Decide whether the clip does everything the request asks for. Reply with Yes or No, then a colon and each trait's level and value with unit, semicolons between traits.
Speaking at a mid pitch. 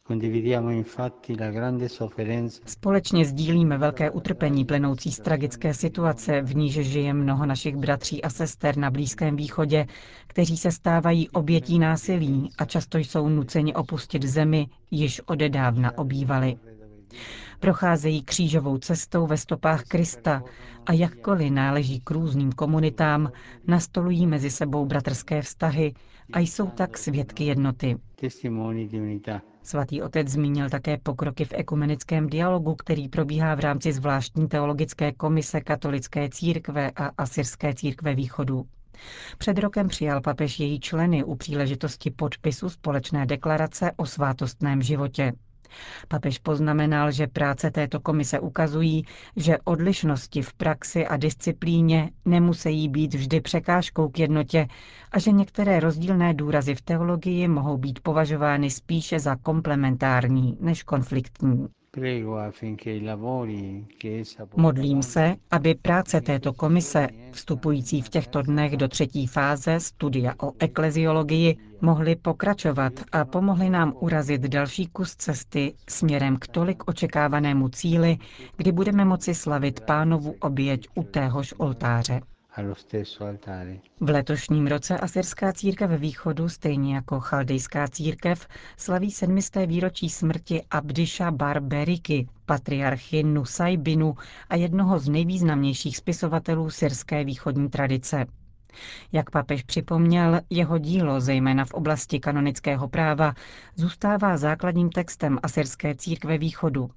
Yes: medium, 150 Hz